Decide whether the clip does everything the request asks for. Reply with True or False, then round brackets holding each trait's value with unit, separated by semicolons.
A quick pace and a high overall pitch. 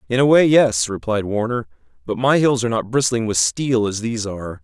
False (220 wpm; 115 Hz)